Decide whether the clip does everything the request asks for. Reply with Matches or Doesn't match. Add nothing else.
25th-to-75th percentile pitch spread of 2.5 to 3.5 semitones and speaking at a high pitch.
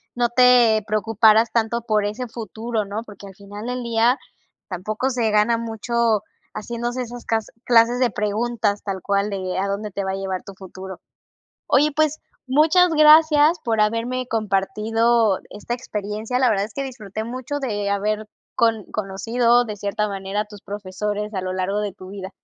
Matches